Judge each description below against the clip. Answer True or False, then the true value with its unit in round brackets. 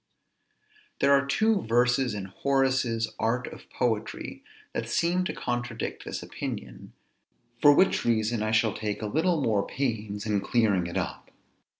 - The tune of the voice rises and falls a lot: False (4.1 semitones)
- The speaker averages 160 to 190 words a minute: False (150 wpm)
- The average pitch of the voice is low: True (115 Hz)